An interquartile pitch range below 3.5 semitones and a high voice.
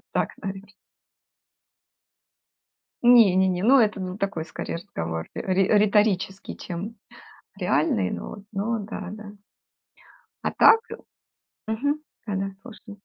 Yes: average, 2.8 semitones; high, 200 Hz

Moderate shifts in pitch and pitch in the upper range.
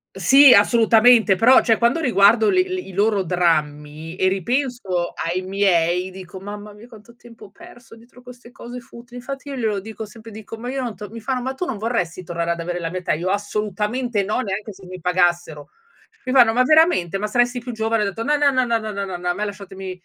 Yes: average, 4.7 semitones; high, 210 Hz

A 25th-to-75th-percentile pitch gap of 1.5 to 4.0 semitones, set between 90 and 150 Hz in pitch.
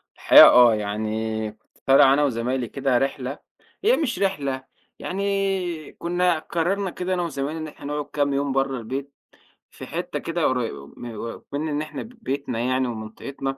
No: average, 5.2 semitones; medium, 140 Hz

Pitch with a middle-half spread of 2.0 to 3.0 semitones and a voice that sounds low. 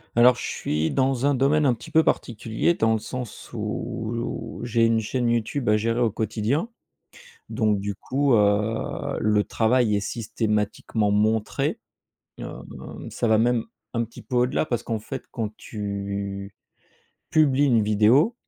Yes: average, 2.7 semitones; low, 115 Hz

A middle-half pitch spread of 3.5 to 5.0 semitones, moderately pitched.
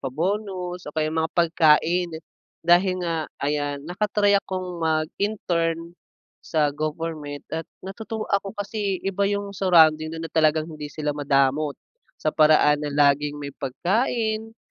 Yes: average, 4.2 semitones; medium, 165 Hz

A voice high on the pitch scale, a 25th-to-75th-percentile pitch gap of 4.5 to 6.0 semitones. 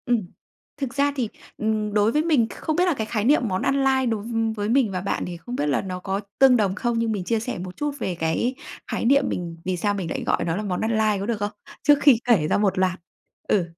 Yes: high, 215 Hz; average, 4.9 semitones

